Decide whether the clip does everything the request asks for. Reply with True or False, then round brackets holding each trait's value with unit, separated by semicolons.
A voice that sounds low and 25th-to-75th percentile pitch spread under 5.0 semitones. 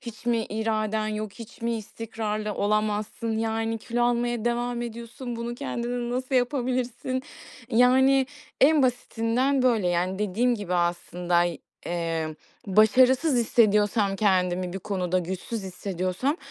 False (225 Hz; 3.6 semitones)